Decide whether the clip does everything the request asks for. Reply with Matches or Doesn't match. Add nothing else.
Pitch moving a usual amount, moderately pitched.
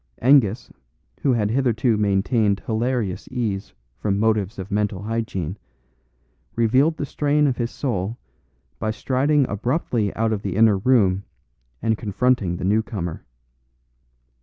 Doesn't match